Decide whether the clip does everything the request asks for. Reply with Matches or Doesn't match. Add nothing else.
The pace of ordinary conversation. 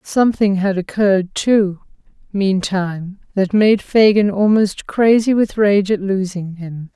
Doesn't match